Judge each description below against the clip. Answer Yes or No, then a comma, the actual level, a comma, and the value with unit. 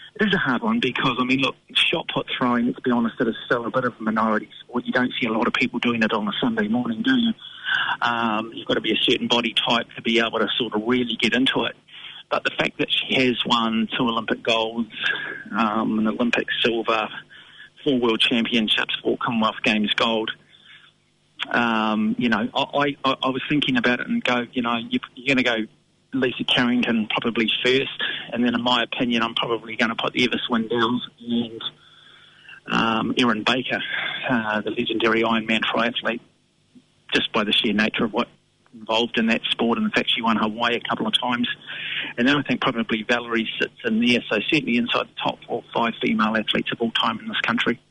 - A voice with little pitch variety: Yes, narrow, 2.0 semitones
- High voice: No, low, 120 Hz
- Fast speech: Yes, fast, 210 wpm